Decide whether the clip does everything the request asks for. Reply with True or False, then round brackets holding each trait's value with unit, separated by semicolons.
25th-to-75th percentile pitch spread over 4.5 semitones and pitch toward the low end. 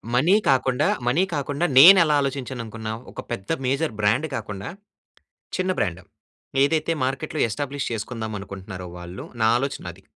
True (5.4 semitones; 130 Hz)